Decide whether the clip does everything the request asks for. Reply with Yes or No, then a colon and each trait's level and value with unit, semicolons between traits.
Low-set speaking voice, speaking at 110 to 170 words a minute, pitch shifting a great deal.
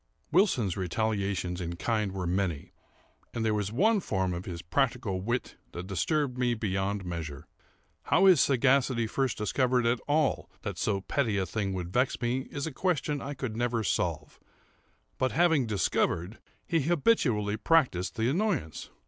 Yes: low, 110 Hz; average, 155 wpm; wide, 6.5 semitones